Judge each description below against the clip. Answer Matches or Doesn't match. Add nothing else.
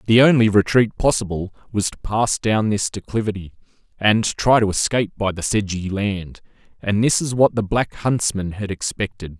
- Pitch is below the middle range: Matches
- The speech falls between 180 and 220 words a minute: Doesn't match